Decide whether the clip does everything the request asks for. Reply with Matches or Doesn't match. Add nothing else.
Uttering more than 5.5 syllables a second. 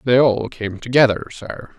Doesn't match